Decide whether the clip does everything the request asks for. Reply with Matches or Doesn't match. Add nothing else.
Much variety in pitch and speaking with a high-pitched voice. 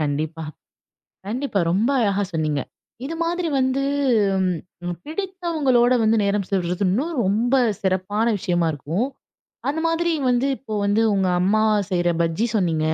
Matches